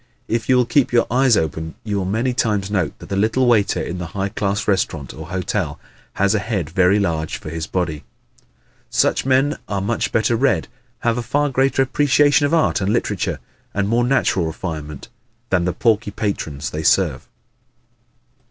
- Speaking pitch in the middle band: No, low, 100 Hz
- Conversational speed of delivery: Yes, average, 180 wpm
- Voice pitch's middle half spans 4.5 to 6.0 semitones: Yes, average, 5.3 semitones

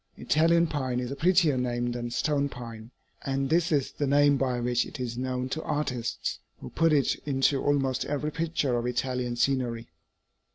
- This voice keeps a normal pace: Yes, average, 175 wpm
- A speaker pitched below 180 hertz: Yes, low, 135 Hz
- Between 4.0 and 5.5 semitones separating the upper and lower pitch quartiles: No, average, 3.0 semitones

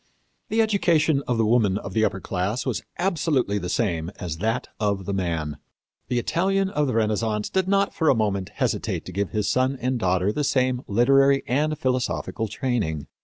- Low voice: Yes, low, 115 Hz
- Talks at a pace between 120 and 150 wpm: No, average, 185 wpm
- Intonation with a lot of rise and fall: Yes, wide, 5.7 semitones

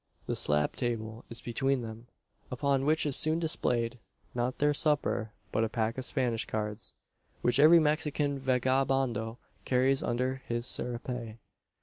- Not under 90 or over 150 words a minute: Yes, average, 140 wpm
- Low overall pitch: Yes, low, 125 Hz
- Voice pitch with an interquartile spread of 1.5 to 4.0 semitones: Yes, average, 3.0 semitones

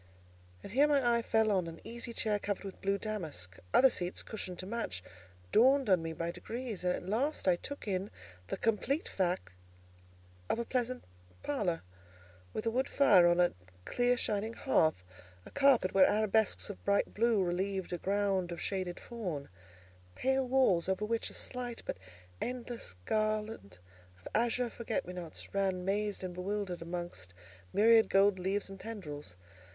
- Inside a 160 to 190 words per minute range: Yes, average, 165 wpm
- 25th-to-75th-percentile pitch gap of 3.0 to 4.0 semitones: No, average, 4.4 semitones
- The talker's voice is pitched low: No, high, 205 Hz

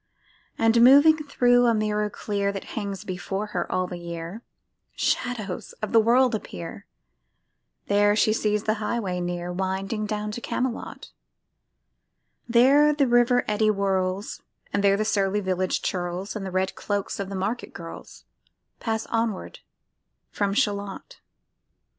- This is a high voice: Yes, high, 205 Hz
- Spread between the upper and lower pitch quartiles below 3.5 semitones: Yes, average, 3.0 semitones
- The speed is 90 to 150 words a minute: Yes, average, 140 wpm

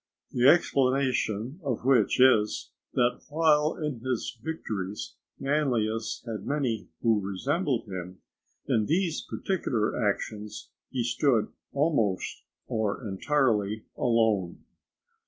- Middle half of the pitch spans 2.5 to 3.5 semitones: No, average, 4.8 semitones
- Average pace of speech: No, slow, 100 wpm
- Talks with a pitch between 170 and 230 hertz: No, low, 120 Hz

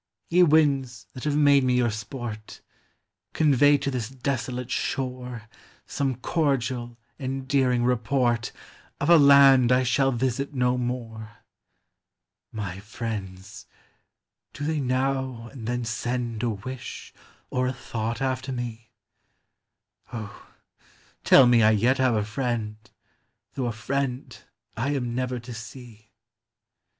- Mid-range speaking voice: No, low, 125 Hz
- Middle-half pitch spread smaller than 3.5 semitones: Yes, narrow, 2.6 semitones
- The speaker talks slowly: Yes, slow, 125 wpm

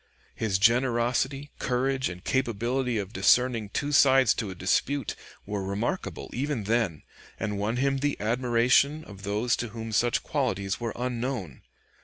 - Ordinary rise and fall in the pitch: Yes, average, 4.1 semitones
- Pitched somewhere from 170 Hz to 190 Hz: No, low, 120 Hz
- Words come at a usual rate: Yes, average, 145 wpm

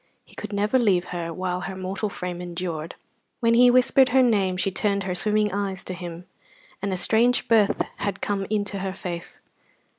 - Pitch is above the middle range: Yes, high, 195 Hz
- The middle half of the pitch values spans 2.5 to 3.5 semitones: Yes, average, 2.8 semitones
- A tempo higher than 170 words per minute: Yes, average, 185 wpm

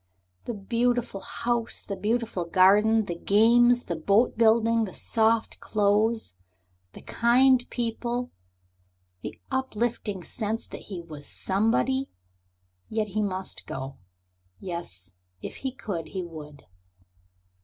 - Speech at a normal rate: No, slow, 115 wpm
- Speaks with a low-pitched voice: No, high, 215 Hz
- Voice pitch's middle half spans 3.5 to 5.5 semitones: Yes, average, 4.2 semitones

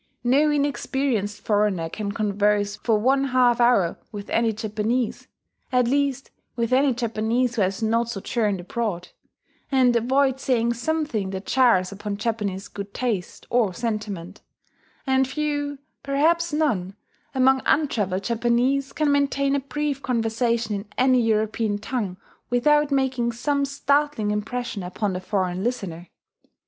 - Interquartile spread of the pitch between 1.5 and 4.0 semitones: No, average, 4.4 semitones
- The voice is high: Yes, high, 235 Hz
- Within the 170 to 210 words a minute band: No, slow, 135 wpm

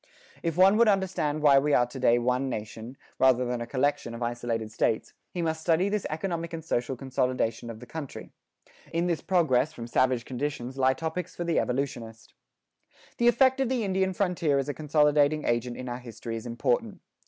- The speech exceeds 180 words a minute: Yes, average, 190 wpm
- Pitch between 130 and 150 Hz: Yes, medium, 140 Hz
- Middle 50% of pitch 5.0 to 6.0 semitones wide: Yes, wide, 5.5 semitones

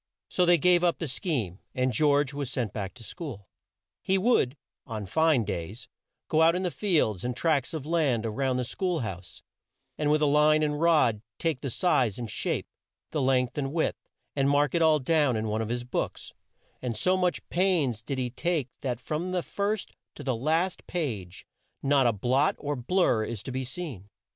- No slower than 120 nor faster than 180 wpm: No, average, 195 wpm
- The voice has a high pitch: No, medium, 140 Hz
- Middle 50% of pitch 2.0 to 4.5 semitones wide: No, average, 5.2 semitones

